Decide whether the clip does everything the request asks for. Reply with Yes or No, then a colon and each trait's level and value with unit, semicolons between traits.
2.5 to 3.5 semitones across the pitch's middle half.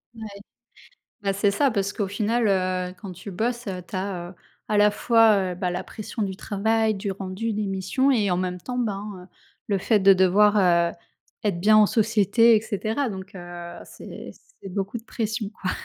Yes: average, 2.8 semitones